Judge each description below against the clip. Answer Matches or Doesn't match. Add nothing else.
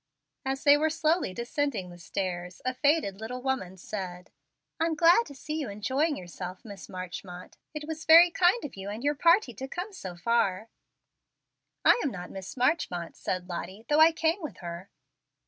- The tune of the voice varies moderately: Doesn't match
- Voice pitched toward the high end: Matches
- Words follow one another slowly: Doesn't match